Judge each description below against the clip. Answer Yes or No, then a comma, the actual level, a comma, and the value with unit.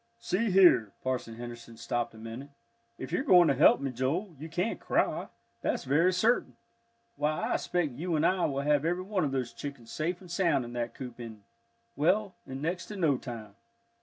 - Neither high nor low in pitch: Yes, medium, 150 Hz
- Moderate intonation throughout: No, wide, 6.6 semitones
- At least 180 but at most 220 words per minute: Yes, average, 195 wpm